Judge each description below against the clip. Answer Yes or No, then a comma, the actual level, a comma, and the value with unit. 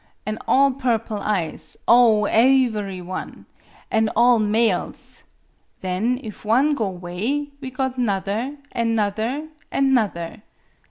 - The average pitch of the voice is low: No, high, 225 Hz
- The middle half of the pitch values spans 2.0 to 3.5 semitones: No, average, 3.9 semitones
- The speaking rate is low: Yes, slow, 120 wpm